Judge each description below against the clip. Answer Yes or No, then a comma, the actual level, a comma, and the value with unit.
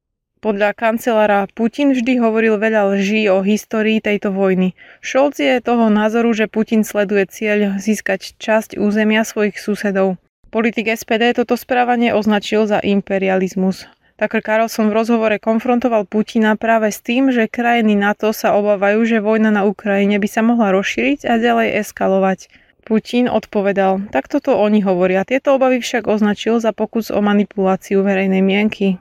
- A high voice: Yes, high, 215 Hz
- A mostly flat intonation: Yes, narrow, 2.2 semitones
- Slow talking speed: No, average, 150 wpm